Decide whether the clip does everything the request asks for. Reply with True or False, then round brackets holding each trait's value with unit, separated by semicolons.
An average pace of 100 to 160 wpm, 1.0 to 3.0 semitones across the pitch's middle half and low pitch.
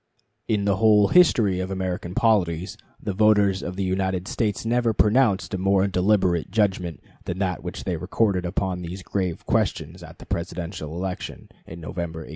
False (170 wpm; 2.5 semitones; 95 Hz)